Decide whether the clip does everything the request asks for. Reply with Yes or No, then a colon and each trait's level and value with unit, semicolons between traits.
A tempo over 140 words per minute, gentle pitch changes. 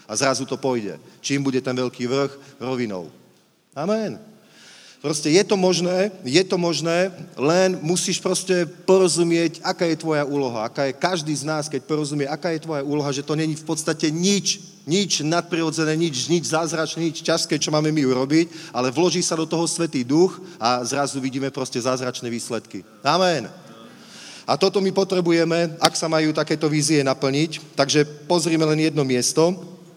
No: fast, 165 wpm; average, 3.8 semitones